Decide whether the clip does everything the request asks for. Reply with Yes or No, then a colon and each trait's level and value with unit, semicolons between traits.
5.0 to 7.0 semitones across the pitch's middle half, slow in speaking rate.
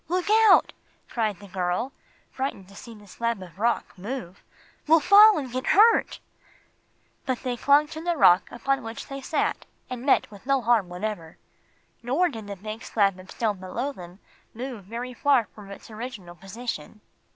No: wide, 5.5 semitones; average, 175 wpm